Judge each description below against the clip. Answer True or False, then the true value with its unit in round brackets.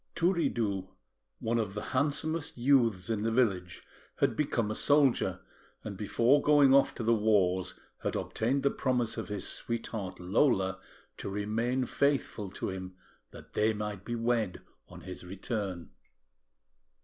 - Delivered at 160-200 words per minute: False (145 wpm)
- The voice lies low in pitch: True (110 Hz)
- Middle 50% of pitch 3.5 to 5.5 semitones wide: True (4.8 semitones)